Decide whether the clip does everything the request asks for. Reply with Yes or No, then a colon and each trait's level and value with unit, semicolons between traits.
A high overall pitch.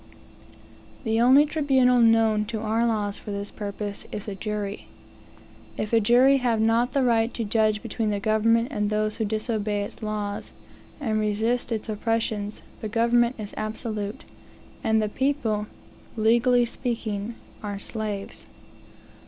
Yes: high, 220 Hz